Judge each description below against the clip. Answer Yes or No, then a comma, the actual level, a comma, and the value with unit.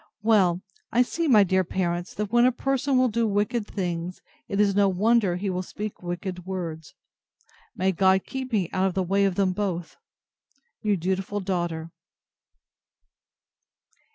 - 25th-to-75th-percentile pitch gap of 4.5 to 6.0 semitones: No, average, 2.8 semitones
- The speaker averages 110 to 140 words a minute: No, average, 155 wpm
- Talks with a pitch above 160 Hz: Yes, high, 190 Hz